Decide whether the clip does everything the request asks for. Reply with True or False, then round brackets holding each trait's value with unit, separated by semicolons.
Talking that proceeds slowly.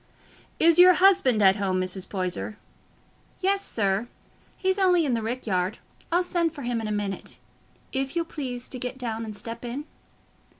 False (175 wpm)